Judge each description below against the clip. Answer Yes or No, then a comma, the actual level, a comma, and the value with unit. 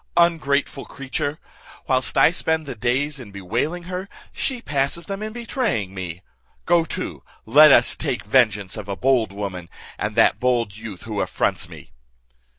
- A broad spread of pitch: Yes, wide, 7.5 semitones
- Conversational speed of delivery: Yes, average, 155 wpm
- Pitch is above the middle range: No, low, 130 Hz